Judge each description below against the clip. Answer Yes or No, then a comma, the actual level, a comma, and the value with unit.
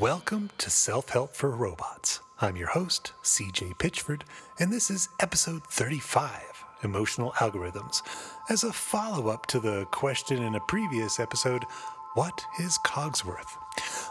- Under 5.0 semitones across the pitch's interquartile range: No, average, 5.3 semitones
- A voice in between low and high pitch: Yes, medium, 150 Hz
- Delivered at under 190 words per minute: Yes, slow, 135 wpm